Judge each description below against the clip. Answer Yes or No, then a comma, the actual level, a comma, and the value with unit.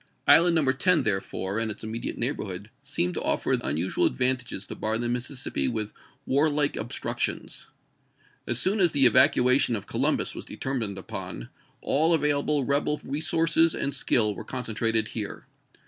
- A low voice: Yes, low, 125 Hz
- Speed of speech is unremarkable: Yes, average, 160 wpm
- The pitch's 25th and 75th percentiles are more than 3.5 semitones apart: Yes, average, 5.0 semitones